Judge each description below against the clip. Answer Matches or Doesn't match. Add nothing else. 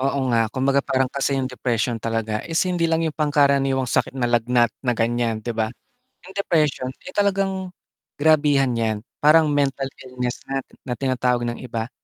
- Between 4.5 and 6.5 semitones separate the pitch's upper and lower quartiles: Doesn't match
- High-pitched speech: Doesn't match